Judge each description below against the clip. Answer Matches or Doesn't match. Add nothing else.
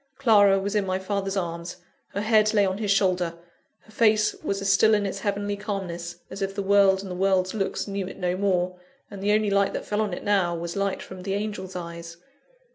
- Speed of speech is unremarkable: Doesn't match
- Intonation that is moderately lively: Doesn't match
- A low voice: Doesn't match